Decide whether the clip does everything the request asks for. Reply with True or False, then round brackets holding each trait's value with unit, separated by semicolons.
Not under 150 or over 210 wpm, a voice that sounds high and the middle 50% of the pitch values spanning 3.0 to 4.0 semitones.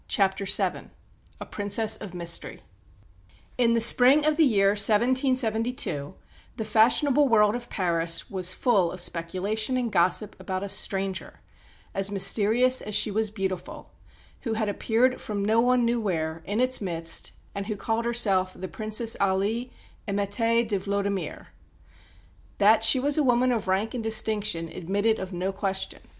True (155 wpm; 210 Hz; 3.4 semitones)